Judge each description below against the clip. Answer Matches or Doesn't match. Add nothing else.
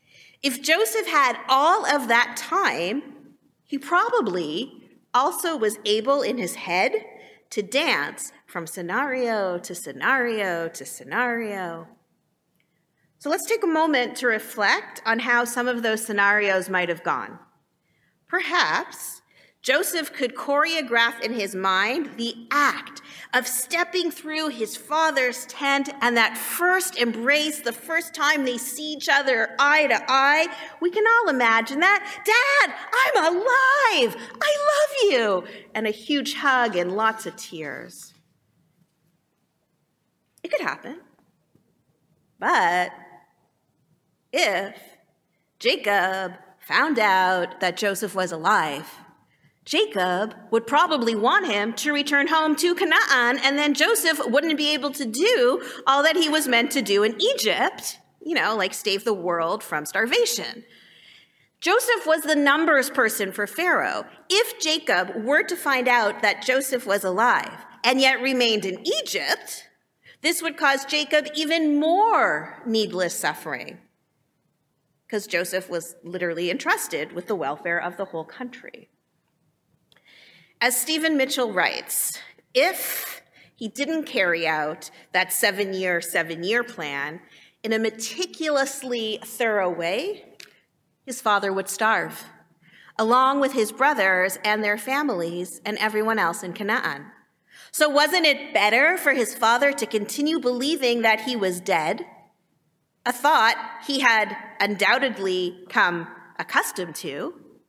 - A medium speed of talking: Doesn't match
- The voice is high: Matches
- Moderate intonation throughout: Doesn't match